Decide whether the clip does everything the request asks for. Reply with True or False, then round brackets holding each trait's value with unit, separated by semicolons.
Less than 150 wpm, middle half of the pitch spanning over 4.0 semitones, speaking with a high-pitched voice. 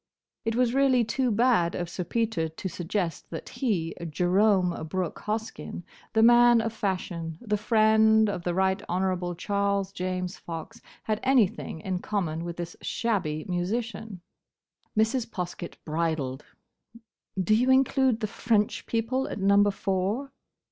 True (140 wpm; 4.4 semitones; 200 Hz)